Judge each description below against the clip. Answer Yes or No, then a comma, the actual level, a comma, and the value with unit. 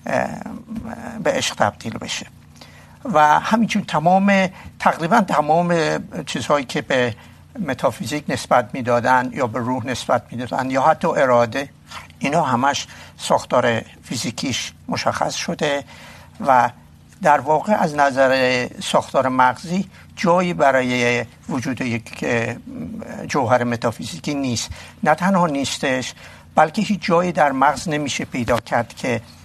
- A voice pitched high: No, low, 135 Hz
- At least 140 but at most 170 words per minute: No, average, 115 wpm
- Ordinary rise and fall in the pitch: No, wide, 5.9 semitones